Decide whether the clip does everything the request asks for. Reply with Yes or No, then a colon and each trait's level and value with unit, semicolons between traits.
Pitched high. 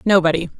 No: medium, 180 Hz